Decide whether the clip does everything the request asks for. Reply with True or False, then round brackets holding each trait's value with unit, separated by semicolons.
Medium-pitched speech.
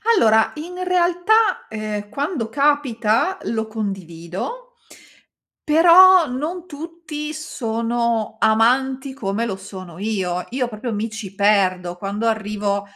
False (230 Hz)